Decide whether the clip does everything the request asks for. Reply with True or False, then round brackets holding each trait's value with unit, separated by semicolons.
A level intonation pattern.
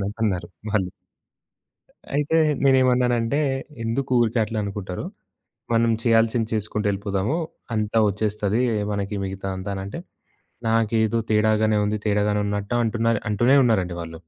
True (2.3 semitones)